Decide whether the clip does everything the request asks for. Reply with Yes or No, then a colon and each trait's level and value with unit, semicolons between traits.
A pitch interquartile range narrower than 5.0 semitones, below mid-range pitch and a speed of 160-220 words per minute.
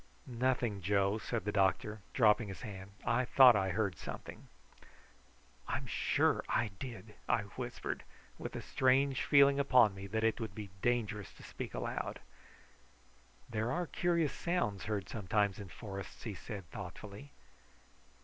No: average, 4.1 semitones; low, 110 Hz; average, 145 wpm